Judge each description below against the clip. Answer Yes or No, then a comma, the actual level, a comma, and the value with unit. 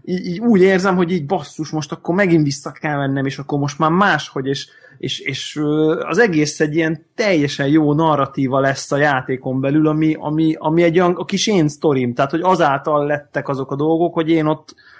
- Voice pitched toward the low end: No, medium, 155 Hz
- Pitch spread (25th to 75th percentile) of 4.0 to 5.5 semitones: No, average, 2.9 semitones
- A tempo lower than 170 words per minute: No, fast, 195 wpm